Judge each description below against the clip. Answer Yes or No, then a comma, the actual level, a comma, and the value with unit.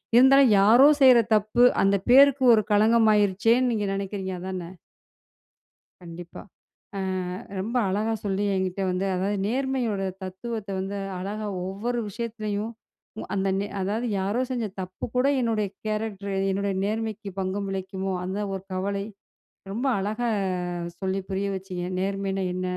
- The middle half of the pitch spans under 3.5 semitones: Yes, average, 2.8 semitones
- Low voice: No, high, 200 Hz